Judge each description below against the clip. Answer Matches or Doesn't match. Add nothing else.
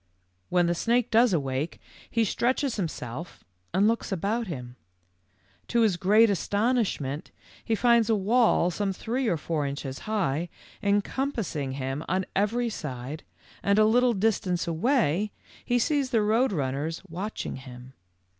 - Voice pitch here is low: Doesn't match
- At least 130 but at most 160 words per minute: Matches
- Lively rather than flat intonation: Matches